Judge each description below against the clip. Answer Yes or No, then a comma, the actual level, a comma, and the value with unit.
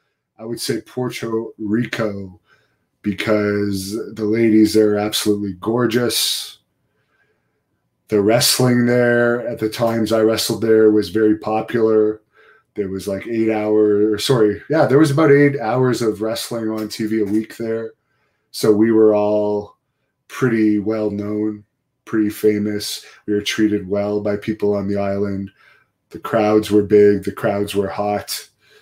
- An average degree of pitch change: No, narrow, 1.4 semitones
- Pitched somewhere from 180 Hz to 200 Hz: No, low, 110 Hz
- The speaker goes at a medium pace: Yes, average, 145 wpm